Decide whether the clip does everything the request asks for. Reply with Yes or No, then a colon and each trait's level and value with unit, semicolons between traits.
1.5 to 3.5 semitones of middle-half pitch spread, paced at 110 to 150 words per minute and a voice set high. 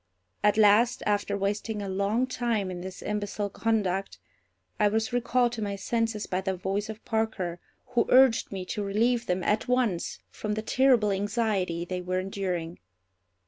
No: average, 3.0 semitones; average, 165 wpm; high, 210 Hz